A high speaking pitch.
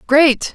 Yes: very high, 280 Hz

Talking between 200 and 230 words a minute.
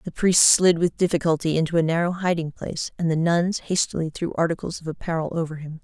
Yes: fast, 205 wpm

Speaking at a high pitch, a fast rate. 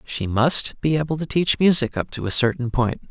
No: low, 135 Hz; fast, 230 wpm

